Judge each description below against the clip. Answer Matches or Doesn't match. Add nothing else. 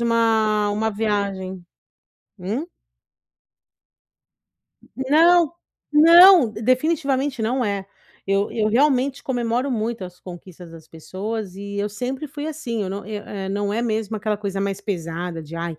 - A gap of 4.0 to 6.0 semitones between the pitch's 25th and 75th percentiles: Matches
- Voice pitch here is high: Matches